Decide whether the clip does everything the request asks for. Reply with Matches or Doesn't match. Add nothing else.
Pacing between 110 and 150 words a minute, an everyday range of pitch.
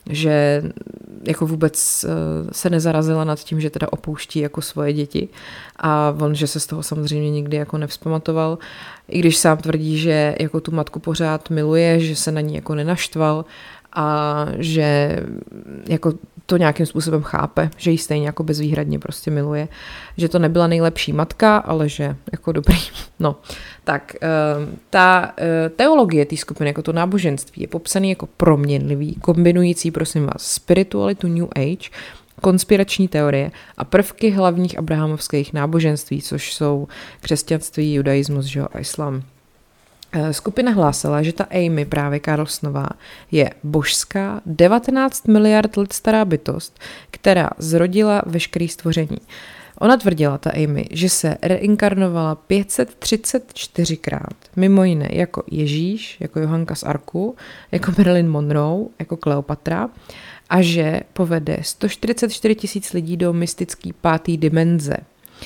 Matches